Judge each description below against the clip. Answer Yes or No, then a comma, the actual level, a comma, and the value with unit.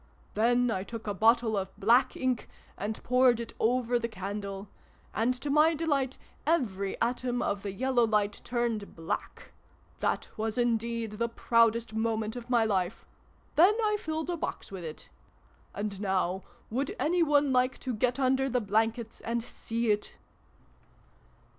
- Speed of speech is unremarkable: Yes, average, 155 wpm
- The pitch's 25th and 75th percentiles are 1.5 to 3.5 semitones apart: Yes, average, 3.1 semitones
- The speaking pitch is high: Yes, high, 230 Hz